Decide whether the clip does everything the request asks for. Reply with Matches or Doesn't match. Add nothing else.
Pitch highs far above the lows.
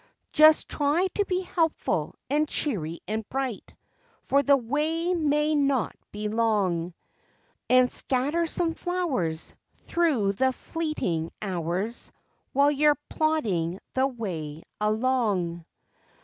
Matches